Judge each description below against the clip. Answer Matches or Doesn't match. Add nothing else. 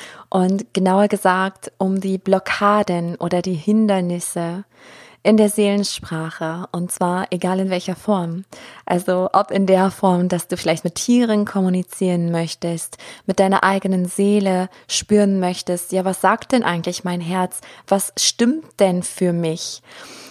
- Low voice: Doesn't match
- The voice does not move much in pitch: Matches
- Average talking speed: Matches